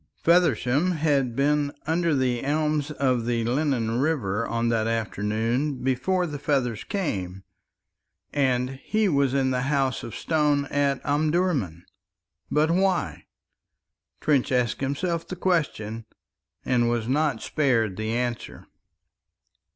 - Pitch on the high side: No, low, 135 Hz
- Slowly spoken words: Yes, slow, 120 wpm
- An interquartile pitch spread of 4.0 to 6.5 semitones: Yes, average, 4.5 semitones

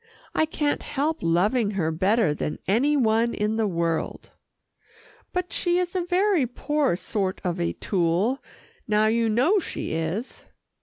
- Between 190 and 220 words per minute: No, average, 150 wpm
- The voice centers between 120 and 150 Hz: No, high, 225 Hz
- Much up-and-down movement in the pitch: Yes, wide, 8.0 semitones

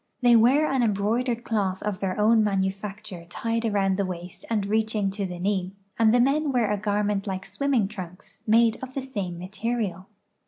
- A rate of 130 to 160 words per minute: No, average, 185 wpm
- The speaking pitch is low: No, high, 210 Hz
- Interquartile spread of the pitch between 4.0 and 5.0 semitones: No, average, 3.2 semitones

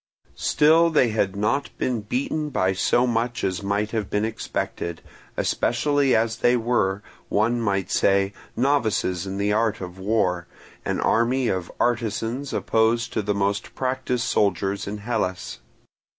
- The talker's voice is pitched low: Yes, low, 110 Hz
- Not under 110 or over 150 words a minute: Yes, average, 145 wpm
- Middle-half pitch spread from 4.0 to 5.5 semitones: No, average, 3.6 semitones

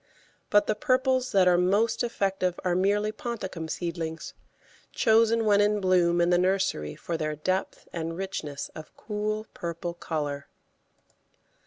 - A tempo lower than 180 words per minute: Yes, average, 140 wpm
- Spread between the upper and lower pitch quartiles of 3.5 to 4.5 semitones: Yes, average, 3.8 semitones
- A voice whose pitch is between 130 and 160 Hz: No, medium, 185 Hz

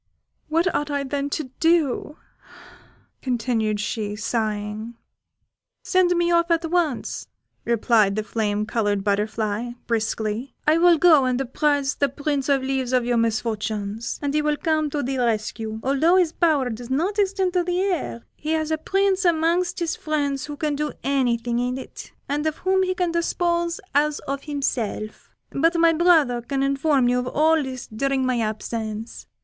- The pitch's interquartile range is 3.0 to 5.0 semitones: No, wide, 5.6 semitones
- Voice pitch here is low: No, very high, 275 Hz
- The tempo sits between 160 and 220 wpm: Yes, average, 165 wpm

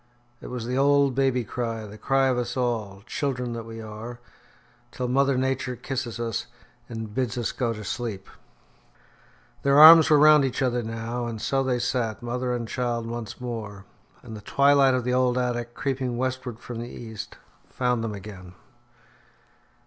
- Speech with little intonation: Yes, narrow, 2.3 semitones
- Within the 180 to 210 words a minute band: No, average, 170 wpm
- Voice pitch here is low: Yes, low, 120 Hz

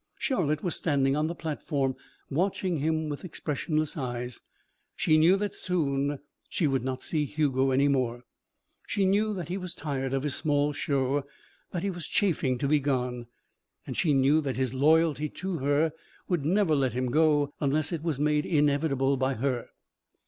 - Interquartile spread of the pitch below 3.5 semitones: Yes, average, 3.1 semitones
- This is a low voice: No, medium, 145 Hz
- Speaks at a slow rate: No, average, 175 wpm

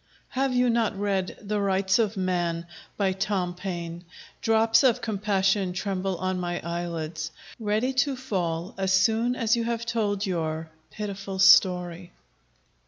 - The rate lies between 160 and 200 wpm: No, average, 140 wpm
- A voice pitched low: No, high, 195 Hz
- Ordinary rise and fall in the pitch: Yes, average, 3.7 semitones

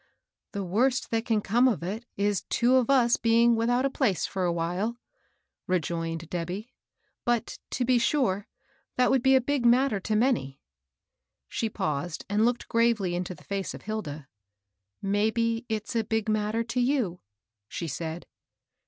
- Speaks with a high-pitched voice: Yes, high, 220 Hz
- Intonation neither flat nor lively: Yes, average, 4.9 semitones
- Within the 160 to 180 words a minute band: Yes, average, 170 wpm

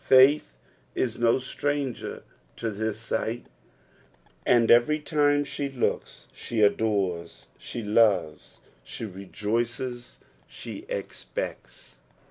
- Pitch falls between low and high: No, low, 120 Hz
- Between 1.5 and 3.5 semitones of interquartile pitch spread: No, average, 3.9 semitones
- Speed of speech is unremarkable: No, slow, 100 wpm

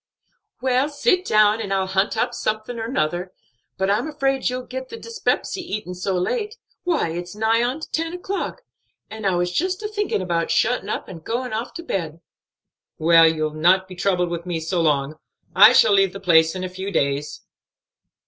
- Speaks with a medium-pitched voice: No, high, 200 Hz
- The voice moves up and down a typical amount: No, wide, 6.6 semitones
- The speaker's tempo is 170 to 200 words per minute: Yes, average, 190 wpm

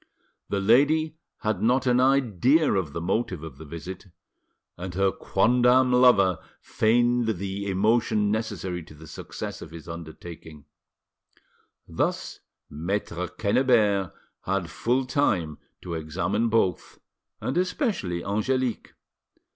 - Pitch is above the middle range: No, low, 100 Hz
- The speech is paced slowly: Yes, slow, 115 wpm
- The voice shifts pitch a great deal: Yes, wide, 6.0 semitones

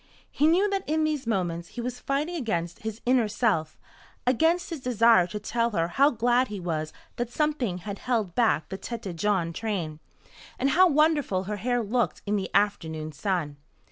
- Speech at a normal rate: Yes, average, 180 wpm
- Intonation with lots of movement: Yes, wide, 6.1 semitones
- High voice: Yes, high, 225 Hz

